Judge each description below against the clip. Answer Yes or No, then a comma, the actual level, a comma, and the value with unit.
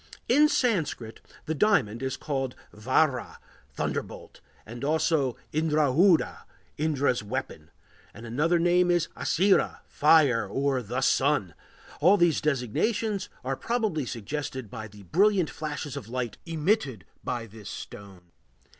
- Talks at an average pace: No, slow, 120 wpm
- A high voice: No, medium, 140 Hz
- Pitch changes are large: Yes, wide, 5.9 semitones